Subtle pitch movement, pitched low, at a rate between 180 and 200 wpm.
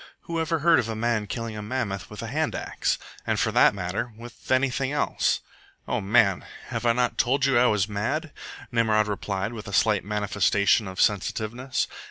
No: average, 3.4 semitones; low, 110 Hz; average, 190 wpm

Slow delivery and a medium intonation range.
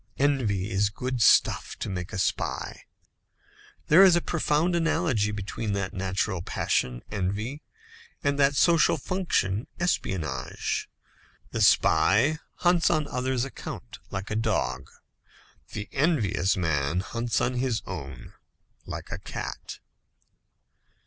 No: slow, 120 wpm; wide, 7.3 semitones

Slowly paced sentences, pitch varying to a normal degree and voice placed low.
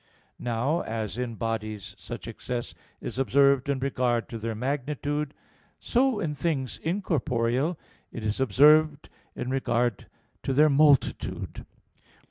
Yes: slow, 120 wpm; average, 4.1 semitones; low, 130 Hz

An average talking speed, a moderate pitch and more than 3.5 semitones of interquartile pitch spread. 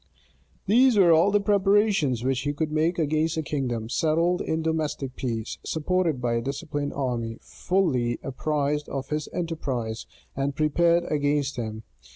Yes: average, 150 wpm; medium, 150 Hz; average, 4.3 semitones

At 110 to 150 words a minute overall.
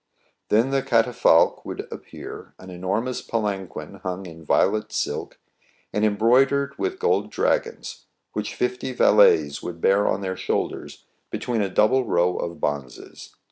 Yes: average, 140 wpm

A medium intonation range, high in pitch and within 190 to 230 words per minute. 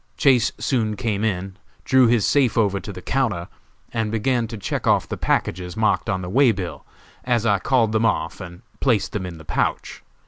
No: average, 4.1 semitones; low, 110 Hz; average, 200 wpm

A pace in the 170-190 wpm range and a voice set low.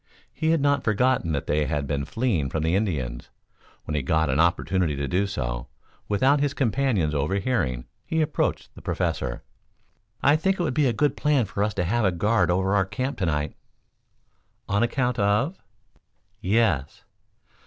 Yes: average, 175 wpm; low, 100 Hz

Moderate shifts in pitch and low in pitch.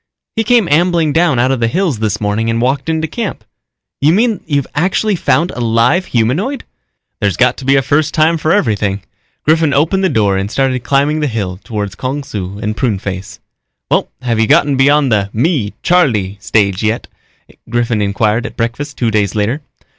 No: wide, 6.6 semitones; low, 130 Hz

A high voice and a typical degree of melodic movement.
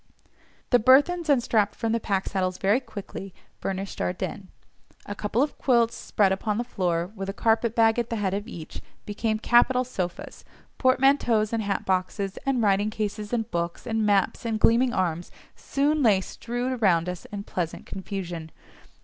Yes: high, 210 Hz; average, 3.7 semitones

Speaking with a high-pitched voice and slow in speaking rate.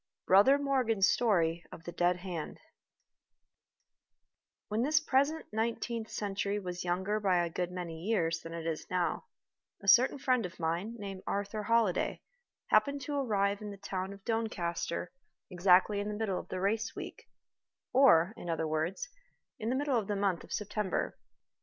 No: high, 200 Hz; average, 165 wpm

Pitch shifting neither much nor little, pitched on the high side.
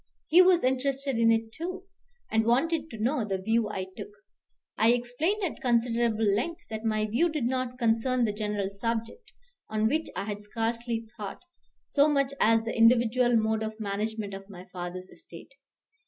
Yes: average, 3.1 semitones; high, 230 Hz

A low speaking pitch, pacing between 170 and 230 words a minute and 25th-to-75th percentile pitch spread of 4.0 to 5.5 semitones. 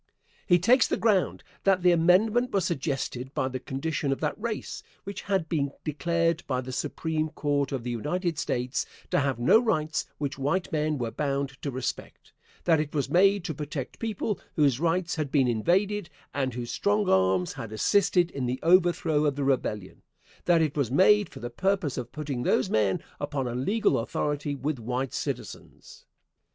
No: medium, 150 Hz; average, 180 wpm; average, 5.1 semitones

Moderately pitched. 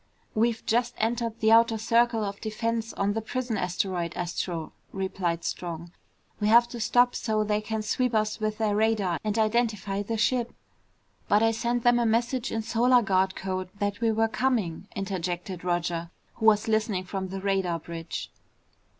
No: high, 215 Hz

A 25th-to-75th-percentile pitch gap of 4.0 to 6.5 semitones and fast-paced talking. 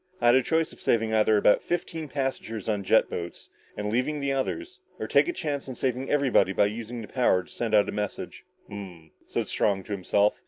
Yes: average, 4.9 semitones; fast, 225 wpm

